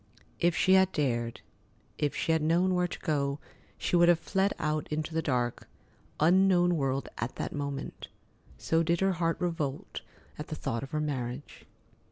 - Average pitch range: Yes, average, 4.0 semitones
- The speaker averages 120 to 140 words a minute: No, average, 175 wpm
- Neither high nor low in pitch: Yes, medium, 155 Hz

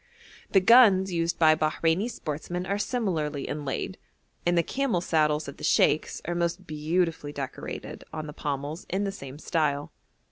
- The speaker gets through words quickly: No, average, 155 wpm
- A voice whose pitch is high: No, medium, 165 Hz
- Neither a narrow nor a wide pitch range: Yes, average, 3.6 semitones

